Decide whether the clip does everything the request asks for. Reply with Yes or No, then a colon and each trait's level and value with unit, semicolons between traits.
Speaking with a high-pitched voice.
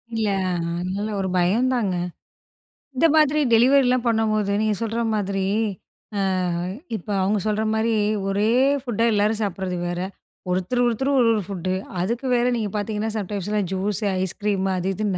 Yes: high, 210 Hz